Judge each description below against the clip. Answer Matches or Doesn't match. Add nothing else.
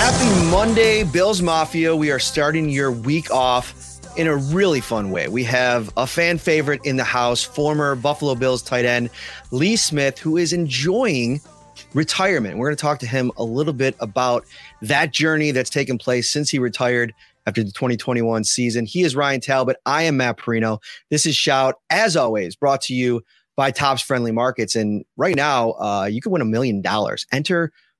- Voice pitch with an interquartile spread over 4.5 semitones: Doesn't match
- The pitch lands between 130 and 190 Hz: Matches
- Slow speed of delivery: Doesn't match